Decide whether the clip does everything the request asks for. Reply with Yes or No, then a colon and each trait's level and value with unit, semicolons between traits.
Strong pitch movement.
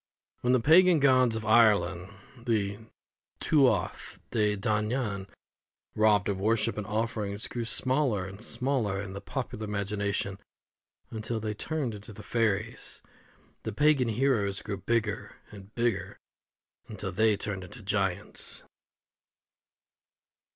No: average, 2.8 semitones